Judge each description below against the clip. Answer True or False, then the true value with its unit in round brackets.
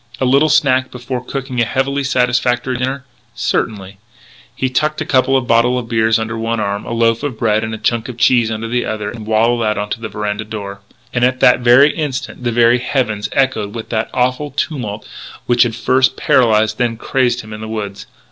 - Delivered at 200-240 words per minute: True (205 wpm)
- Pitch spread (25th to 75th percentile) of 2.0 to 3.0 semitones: True (2.7 semitones)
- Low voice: True (120 Hz)